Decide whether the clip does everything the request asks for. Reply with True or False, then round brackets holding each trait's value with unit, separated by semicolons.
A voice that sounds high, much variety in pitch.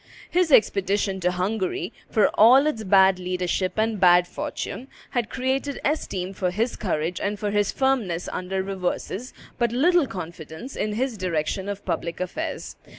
False (200 Hz; 4.8 semitones)